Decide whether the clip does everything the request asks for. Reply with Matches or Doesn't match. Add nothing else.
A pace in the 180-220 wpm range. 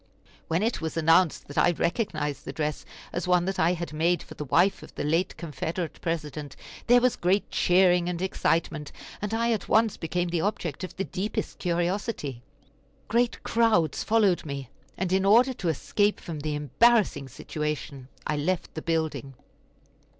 Doesn't match